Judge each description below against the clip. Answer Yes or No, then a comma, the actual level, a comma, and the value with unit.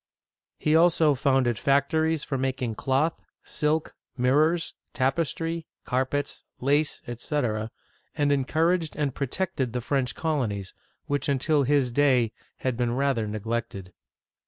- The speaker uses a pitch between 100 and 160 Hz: Yes, medium, 140 Hz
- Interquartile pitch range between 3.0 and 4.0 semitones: Yes, average, 3.6 semitones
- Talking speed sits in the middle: No, slow, 125 wpm